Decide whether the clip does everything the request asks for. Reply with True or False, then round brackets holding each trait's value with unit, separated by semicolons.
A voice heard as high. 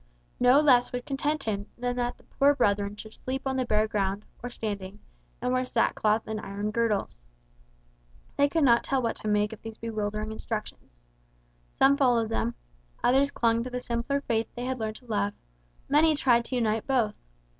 True (235 Hz)